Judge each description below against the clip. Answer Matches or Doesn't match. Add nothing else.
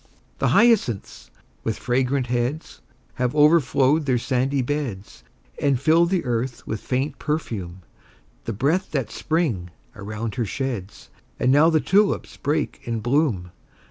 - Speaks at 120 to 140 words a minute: Matches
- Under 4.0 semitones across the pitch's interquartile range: Doesn't match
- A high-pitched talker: Doesn't match